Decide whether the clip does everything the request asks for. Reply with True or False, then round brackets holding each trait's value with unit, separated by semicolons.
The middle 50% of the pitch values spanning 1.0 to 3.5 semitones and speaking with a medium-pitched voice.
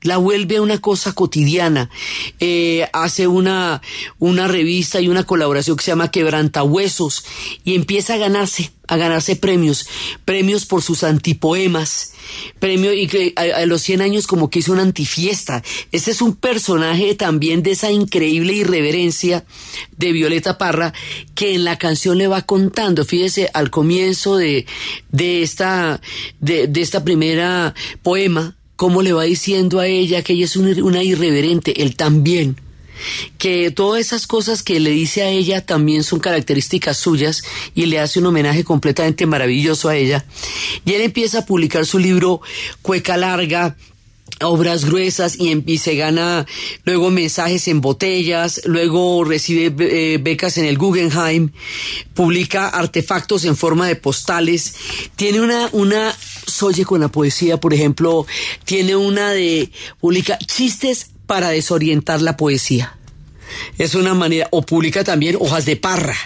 True (2.8 semitones; 170 Hz)